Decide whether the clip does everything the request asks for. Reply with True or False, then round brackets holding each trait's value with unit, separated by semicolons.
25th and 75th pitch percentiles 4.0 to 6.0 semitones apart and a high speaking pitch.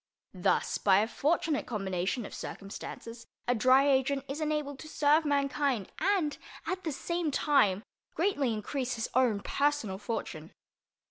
True (4.9 semitones; 275 Hz)